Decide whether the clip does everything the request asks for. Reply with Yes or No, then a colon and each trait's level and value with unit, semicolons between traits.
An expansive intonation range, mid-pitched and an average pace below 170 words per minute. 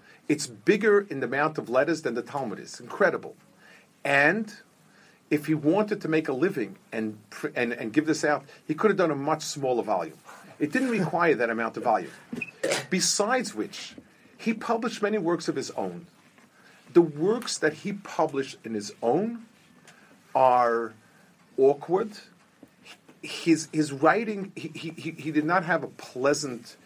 Yes: wide, 6.0 semitones; medium, 165 Hz; average, 160 wpm